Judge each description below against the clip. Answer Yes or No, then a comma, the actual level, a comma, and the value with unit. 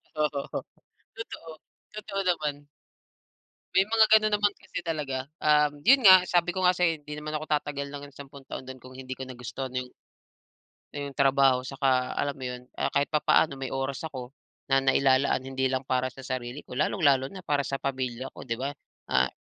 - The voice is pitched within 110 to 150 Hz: Yes, medium, 140 Hz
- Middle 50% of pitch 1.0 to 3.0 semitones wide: Yes, average, 2.7 semitones